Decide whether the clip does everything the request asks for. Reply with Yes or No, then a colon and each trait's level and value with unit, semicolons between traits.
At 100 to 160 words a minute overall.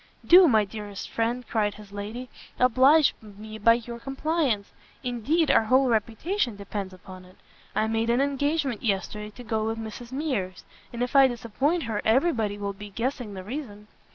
No: average, 175 wpm